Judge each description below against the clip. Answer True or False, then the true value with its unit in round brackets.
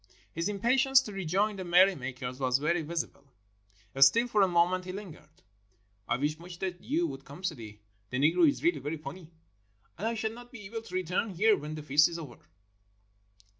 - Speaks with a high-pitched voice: False (180 Hz)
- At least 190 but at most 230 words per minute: True (195 wpm)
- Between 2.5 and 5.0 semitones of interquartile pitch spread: False (5.6 semitones)